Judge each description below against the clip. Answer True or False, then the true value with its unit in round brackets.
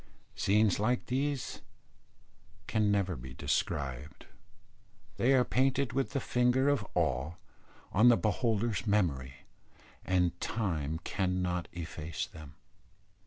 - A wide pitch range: True (7.2 semitones)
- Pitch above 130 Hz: False (100 Hz)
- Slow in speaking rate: True (110 wpm)